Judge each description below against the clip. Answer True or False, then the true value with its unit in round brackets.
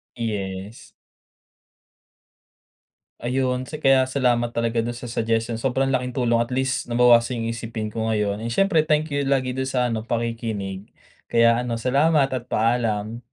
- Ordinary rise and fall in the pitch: False (2.3 semitones)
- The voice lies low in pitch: True (120 Hz)